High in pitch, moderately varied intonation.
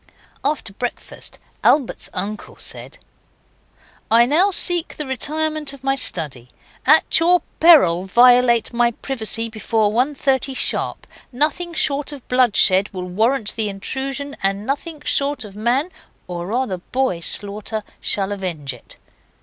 No: high, 245 Hz; wide, 5.7 semitones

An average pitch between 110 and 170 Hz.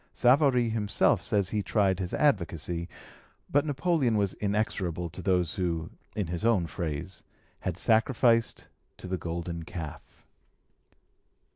No: very low, 95 Hz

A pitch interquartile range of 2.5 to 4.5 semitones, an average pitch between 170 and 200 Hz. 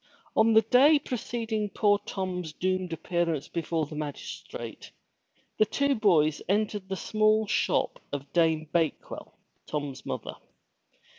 No: average, 5.3 semitones; medium, 185 Hz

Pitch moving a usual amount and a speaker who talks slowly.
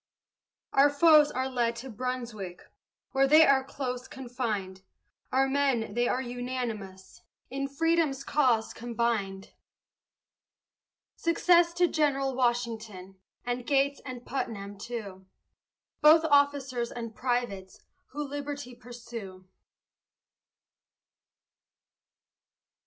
Yes: average, 3.4 semitones; slow, 95 wpm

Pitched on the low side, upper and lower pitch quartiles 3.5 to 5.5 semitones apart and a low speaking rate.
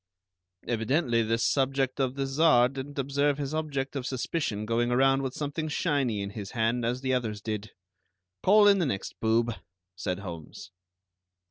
No: low, 130 Hz; average, 3.8 semitones; average, 160 wpm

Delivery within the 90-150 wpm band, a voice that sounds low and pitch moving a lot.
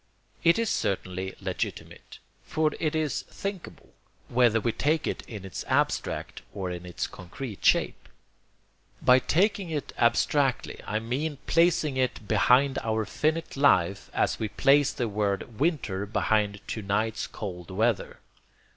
Yes: average, 140 wpm; low, 115 Hz; wide, 6.7 semitones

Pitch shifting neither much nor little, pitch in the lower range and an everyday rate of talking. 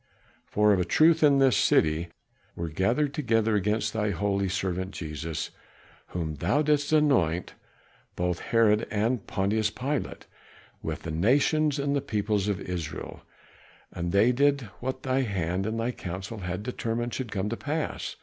No: wide, 6.1 semitones; low, 105 Hz; average, 155 wpm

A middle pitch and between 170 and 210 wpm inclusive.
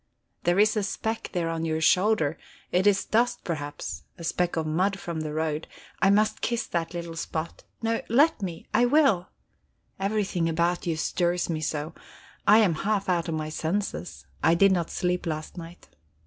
Yes: medium, 175 Hz; average, 180 wpm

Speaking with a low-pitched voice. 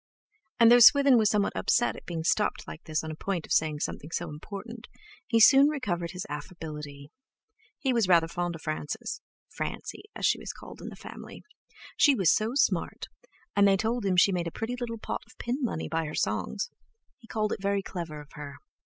No: high, 195 Hz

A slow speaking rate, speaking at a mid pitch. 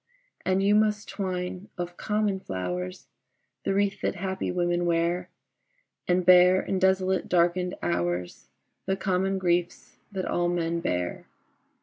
Yes: slow, 130 wpm; medium, 180 Hz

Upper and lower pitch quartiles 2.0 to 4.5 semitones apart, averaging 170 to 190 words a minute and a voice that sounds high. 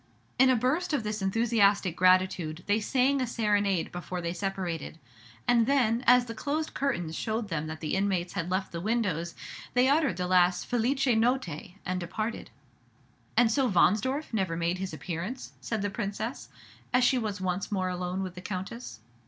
No: average, 5.0 semitones; average, 175 wpm; high, 200 Hz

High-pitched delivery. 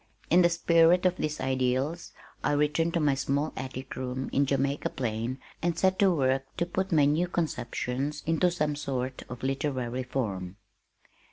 No: medium, 140 Hz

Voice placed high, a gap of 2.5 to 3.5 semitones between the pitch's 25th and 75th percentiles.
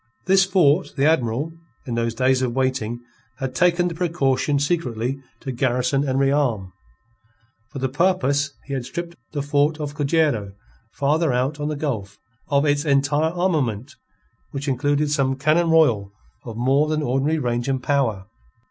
No: medium, 140 Hz; average, 3.2 semitones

